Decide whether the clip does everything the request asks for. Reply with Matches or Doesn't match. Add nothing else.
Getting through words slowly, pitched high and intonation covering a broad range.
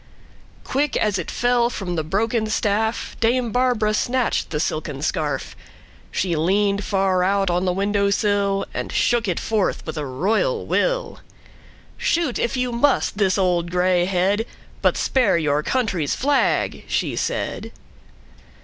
Doesn't match